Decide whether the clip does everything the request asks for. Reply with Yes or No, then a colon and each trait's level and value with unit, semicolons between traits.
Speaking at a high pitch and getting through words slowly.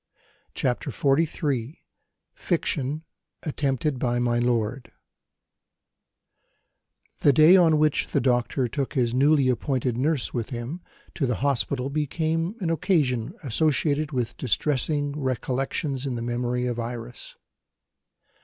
No: low, 135 Hz; slow, 115 wpm